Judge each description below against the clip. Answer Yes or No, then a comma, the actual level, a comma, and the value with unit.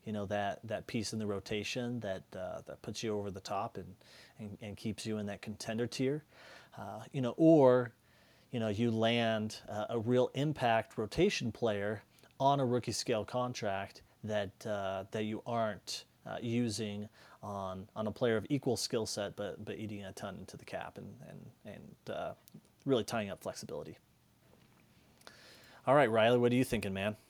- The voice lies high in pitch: No, low, 110 Hz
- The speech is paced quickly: No, average, 180 wpm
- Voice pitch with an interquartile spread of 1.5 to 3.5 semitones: Yes, average, 2.8 semitones